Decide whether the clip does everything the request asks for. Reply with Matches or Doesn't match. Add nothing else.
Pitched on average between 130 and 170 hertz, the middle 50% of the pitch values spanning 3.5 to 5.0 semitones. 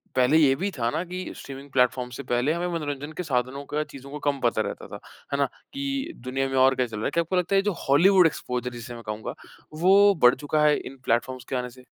Matches